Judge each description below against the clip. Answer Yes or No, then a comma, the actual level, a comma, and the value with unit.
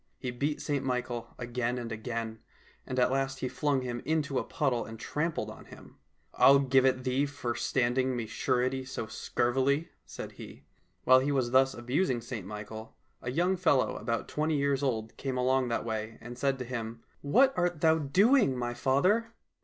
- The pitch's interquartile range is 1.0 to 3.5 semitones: Yes, average, 2.8 semitones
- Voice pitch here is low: Yes, low, 130 Hz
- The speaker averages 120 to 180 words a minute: No, average, 190 wpm